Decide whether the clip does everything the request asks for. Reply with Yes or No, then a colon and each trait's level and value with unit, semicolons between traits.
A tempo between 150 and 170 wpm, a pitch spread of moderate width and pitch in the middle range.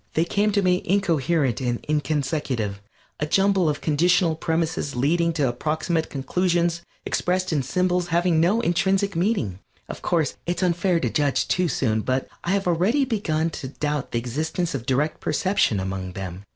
Yes: average, 165 wpm; average, 4.9 semitones; medium, 165 Hz